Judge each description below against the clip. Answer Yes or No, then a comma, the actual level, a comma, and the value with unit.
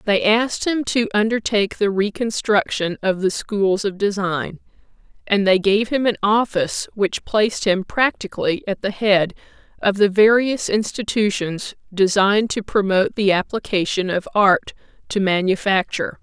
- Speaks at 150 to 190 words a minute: No, average, 140 wpm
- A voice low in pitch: No, high, 205 Hz